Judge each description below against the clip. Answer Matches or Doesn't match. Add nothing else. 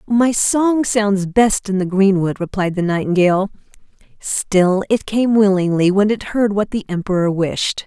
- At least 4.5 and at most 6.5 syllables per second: Doesn't match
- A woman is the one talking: Matches